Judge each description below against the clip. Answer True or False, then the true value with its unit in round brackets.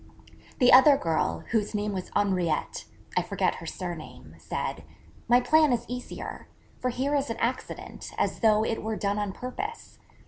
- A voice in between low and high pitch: False (230 Hz)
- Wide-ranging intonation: False (3.8 semitones)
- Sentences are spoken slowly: False (165 wpm)